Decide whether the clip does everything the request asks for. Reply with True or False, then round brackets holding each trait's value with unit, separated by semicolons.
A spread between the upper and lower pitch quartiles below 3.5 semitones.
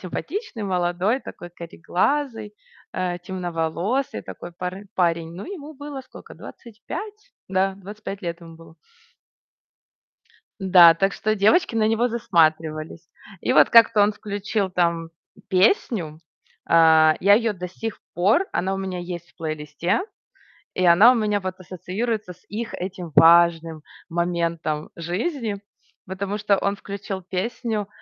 False (4.0 semitones)